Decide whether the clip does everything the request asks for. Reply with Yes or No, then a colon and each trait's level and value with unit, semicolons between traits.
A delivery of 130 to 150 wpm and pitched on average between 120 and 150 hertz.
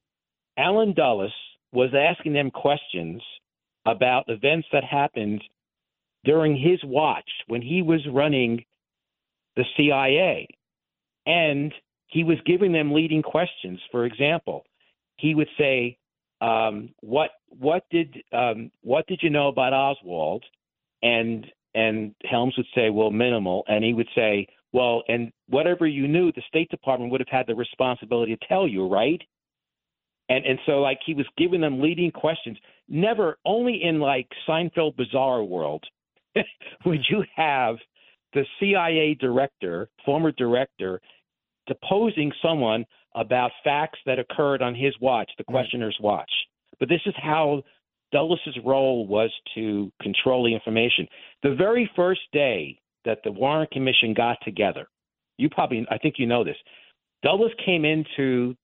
Yes: average, 140 wpm; low, 135 Hz